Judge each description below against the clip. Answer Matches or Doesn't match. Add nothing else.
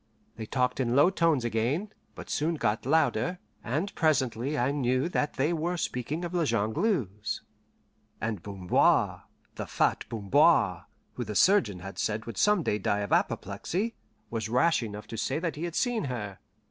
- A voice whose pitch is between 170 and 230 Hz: Doesn't match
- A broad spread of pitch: Matches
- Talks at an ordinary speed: Matches